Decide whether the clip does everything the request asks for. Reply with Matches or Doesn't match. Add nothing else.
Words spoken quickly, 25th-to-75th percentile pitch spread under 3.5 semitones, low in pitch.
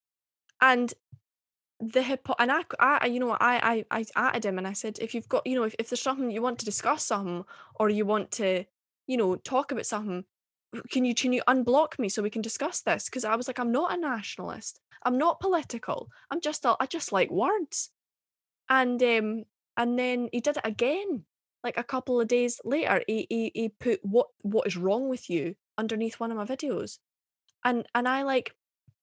Doesn't match